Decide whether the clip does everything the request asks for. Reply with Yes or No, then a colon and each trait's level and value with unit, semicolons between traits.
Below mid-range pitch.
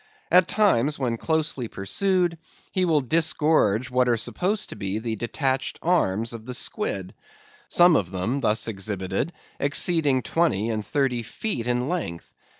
Yes: low, 125 Hz